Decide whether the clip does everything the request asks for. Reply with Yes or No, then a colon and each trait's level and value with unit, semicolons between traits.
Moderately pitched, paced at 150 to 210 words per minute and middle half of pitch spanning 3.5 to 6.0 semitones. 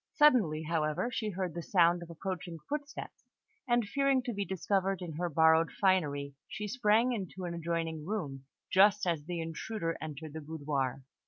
Yes: medium, 175 Hz; average, 165 wpm; average, 4.5 semitones